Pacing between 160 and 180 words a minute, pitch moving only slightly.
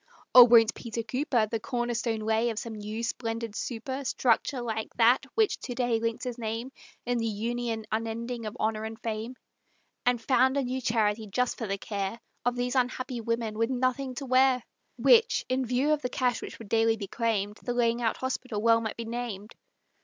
No: average, 200 wpm; narrow, 2.0 semitones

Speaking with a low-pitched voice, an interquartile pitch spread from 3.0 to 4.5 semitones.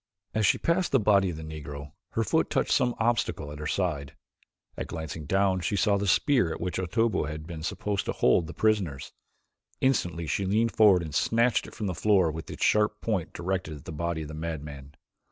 No: very low, 90 Hz; average, 5.2 semitones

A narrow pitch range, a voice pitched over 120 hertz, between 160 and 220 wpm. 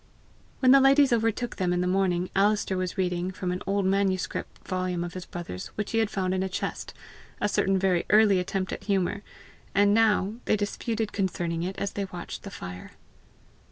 Yes: narrow, 2.3 semitones; high, 190 Hz; average, 190 wpm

